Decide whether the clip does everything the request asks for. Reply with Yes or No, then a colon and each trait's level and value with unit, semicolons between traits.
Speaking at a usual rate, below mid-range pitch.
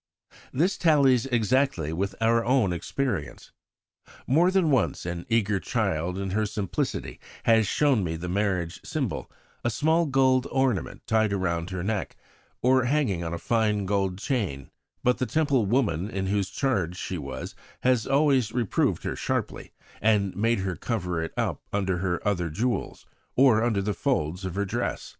Yes: average, 160 wpm; low, 105 Hz